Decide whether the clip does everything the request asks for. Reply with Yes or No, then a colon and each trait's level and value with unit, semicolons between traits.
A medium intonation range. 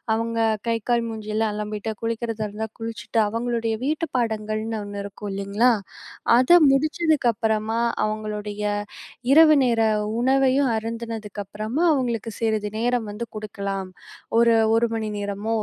No: narrow, 1.9 semitones